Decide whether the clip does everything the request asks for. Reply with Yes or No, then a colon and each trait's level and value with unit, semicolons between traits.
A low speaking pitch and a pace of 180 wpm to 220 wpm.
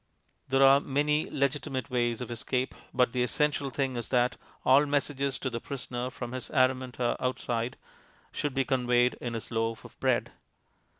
No: low, 130 Hz; average, 165 wpm